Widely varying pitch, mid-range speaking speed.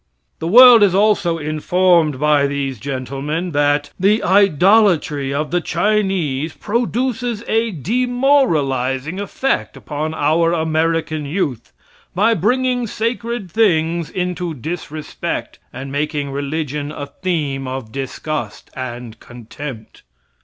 No: wide, 6.0 semitones; slow, 110 wpm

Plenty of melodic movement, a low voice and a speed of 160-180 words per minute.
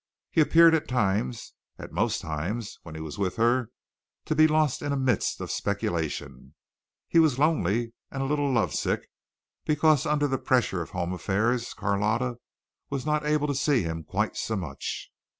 Yes: wide, 7.0 semitones; low, 120 Hz; average, 175 wpm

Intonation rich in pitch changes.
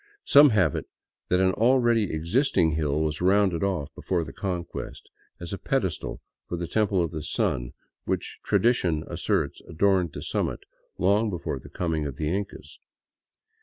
No: average, 4.1 semitones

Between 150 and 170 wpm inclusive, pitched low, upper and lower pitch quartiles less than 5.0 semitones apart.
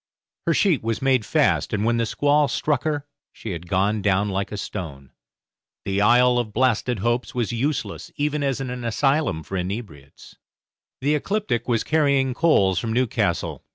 No: average, 165 wpm; low, 120 Hz; wide, 5.4 semitones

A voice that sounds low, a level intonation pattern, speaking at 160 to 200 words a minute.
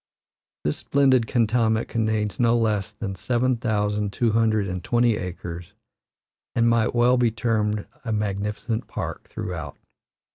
No: low, 110 Hz; narrow, 2.2 semitones; slow, 135 wpm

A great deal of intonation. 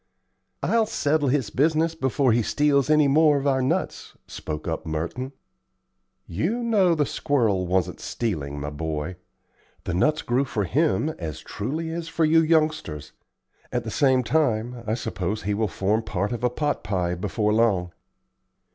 Yes: wide, 8.3 semitones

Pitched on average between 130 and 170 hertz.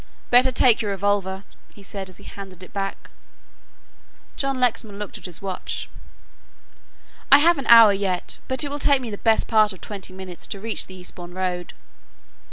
No: high, 200 Hz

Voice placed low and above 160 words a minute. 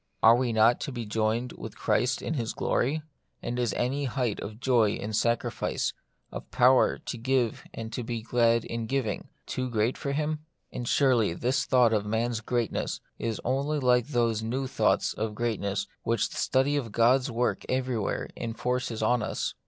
Yes: low, 120 Hz; average, 175 wpm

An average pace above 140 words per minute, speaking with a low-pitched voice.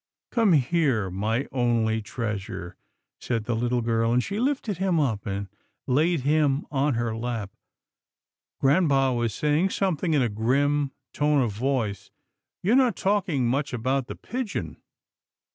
Yes: average, 150 wpm; low, 130 Hz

